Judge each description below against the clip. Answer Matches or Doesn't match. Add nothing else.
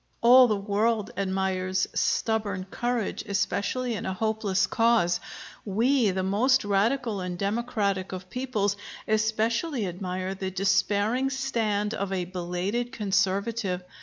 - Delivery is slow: Matches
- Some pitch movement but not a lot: Matches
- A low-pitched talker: Doesn't match